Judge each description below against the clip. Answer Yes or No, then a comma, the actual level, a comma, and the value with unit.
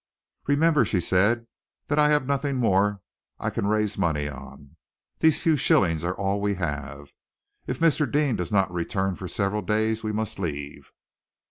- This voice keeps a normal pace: Yes, average, 165 wpm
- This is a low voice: Yes, low, 100 Hz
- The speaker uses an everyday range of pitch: No, wide, 6.4 semitones